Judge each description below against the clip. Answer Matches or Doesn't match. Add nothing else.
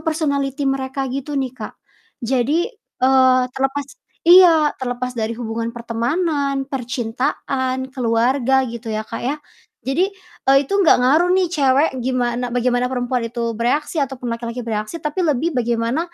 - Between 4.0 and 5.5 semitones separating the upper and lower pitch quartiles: Doesn't match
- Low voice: Doesn't match